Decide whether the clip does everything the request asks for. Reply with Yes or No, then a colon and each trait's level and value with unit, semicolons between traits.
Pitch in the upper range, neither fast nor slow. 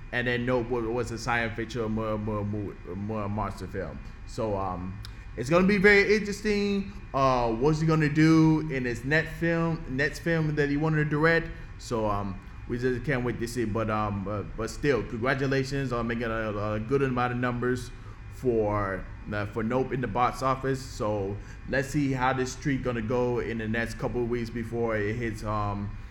No: low, 120 Hz; average, 195 wpm